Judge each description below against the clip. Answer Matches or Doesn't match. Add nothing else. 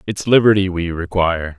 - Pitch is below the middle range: Matches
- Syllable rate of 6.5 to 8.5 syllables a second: Doesn't match